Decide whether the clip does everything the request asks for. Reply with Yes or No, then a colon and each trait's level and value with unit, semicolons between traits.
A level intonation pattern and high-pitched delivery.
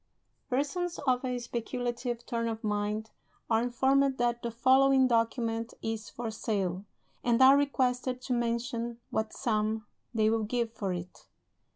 Yes: narrow, 2.3 semitones; high, 235 Hz